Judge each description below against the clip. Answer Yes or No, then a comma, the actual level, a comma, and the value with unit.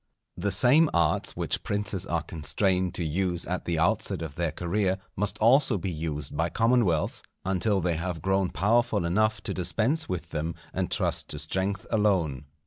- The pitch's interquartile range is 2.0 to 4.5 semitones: Yes, average, 3.7 semitones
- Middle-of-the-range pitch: No, very low, 95 Hz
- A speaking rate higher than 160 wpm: Yes, average, 170 wpm